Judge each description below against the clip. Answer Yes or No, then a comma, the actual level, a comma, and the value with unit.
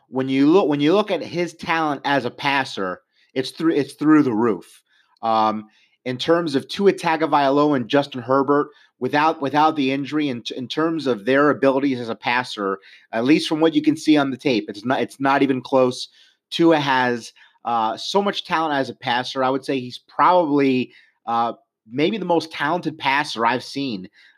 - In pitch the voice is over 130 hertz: Yes, medium, 140 Hz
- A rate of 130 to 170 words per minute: No, average, 195 wpm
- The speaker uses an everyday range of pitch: Yes, average, 3.5 semitones